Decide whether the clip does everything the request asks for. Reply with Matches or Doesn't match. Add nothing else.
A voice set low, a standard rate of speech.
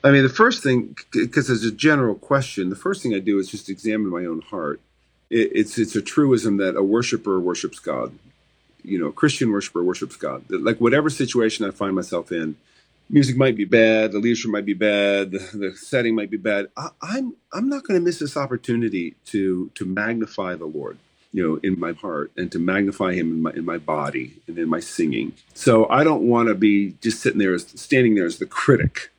Doesn't match